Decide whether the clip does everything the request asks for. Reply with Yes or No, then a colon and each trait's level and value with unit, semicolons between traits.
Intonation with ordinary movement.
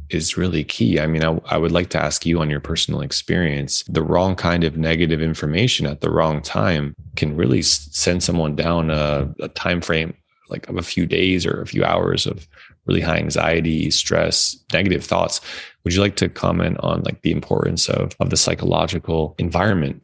No: narrow, 2.1 semitones